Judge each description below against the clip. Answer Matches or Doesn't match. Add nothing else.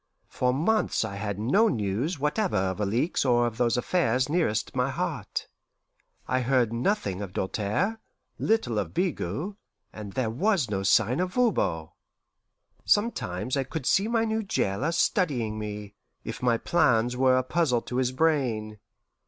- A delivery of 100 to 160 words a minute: Matches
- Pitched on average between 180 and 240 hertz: Doesn't match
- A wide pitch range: Matches